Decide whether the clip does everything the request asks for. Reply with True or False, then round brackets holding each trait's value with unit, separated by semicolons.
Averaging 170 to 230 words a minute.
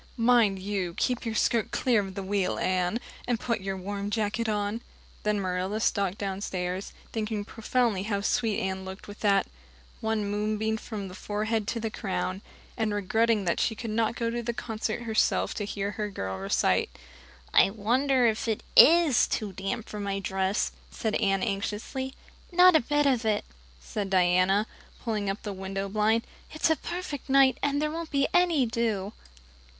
True (175 wpm)